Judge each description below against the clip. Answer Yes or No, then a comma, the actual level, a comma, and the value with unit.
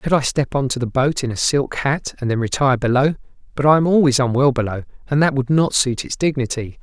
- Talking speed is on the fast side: Yes, fast, 235 wpm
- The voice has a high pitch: No, low, 135 Hz